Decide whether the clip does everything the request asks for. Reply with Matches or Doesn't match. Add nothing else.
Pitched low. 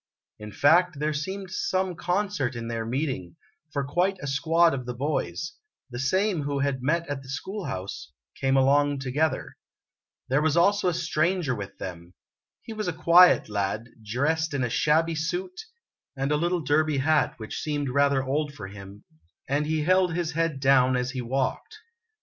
Doesn't match